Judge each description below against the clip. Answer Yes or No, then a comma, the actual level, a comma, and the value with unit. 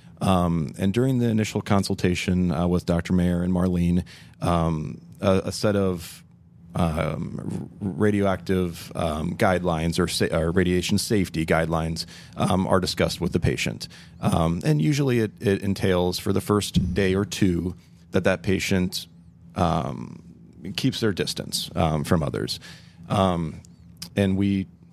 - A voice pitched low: Yes, very low, 90 Hz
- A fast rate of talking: No, average, 140 wpm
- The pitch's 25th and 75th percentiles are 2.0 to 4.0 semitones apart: Yes, narrow, 2.4 semitones